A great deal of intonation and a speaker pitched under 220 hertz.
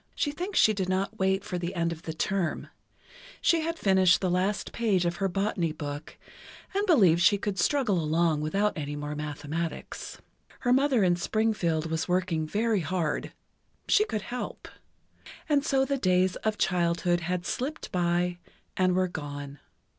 No: average, 4.1 semitones; medium, 185 Hz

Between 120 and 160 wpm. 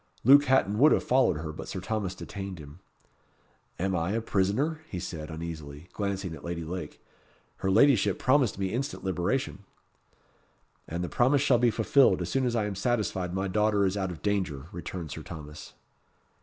No: average, 185 wpm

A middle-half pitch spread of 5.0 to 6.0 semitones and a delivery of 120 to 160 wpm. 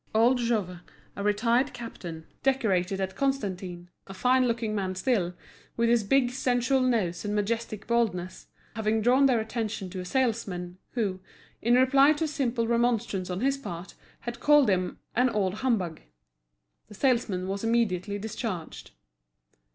No: average, 4.6 semitones; average, 150 wpm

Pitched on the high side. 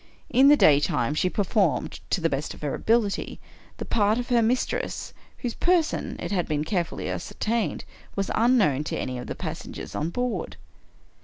Yes: high, 205 Hz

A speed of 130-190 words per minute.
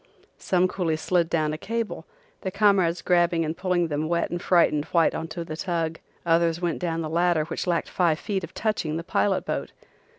No: average, 200 wpm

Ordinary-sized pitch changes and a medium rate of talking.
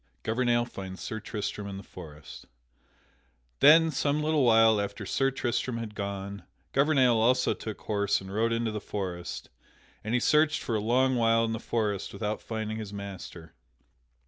Yes: average, 3.5 semitones; average, 170 wpm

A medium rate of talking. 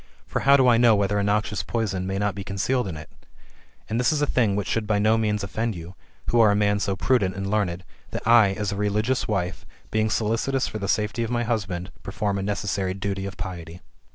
No: fast, 235 wpm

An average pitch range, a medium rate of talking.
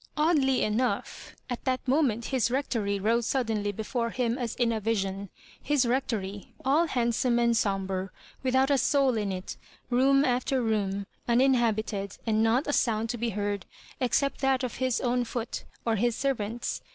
Yes: average, 3.4 semitones; average, 170 wpm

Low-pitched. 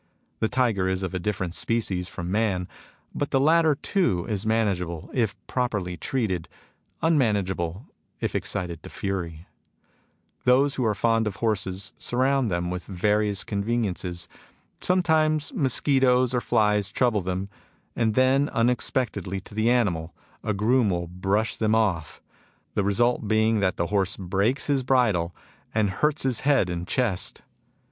Yes: low, 105 Hz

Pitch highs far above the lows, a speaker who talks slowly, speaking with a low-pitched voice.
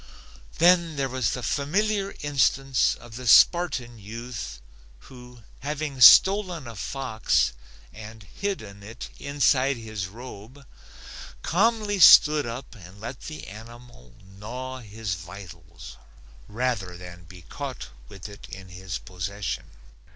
Yes: wide, 6.1 semitones; slow, 120 wpm; low, 120 Hz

